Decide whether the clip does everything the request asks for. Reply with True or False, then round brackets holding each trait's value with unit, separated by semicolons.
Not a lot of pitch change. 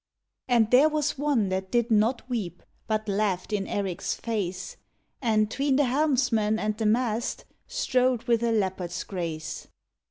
False (4.1 semitones)